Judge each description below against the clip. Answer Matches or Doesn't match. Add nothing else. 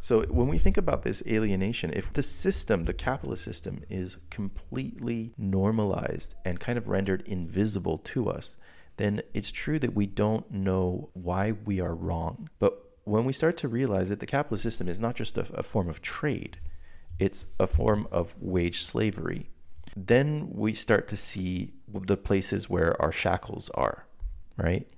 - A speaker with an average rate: Matches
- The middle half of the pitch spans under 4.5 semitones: Matches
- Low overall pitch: Matches